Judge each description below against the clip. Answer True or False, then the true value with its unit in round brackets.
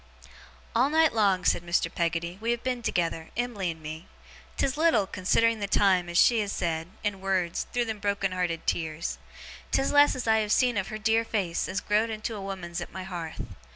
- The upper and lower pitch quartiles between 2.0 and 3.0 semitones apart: False (4.7 semitones)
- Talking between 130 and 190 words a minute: False (205 wpm)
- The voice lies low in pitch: False (195 Hz)